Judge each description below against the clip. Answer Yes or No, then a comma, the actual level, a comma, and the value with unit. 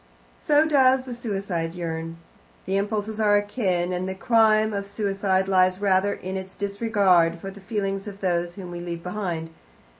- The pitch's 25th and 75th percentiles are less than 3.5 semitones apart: Yes, narrow, 2.6 semitones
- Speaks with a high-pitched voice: Yes, high, 195 Hz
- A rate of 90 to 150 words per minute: No, average, 170 wpm